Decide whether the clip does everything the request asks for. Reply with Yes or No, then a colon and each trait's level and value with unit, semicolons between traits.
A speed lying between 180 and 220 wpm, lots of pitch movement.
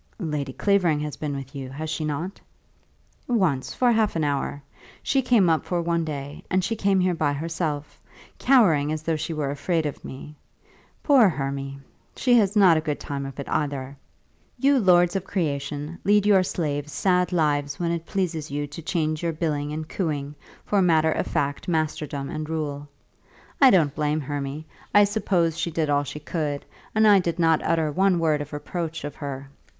No: average, 185 wpm; average, 3.7 semitones